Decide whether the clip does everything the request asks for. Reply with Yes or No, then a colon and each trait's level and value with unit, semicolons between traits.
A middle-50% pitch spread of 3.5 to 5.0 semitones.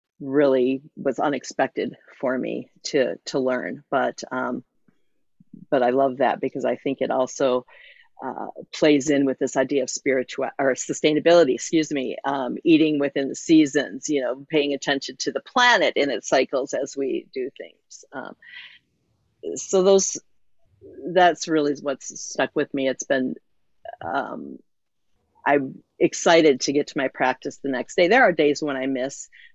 Yes: average, 4.0 semitones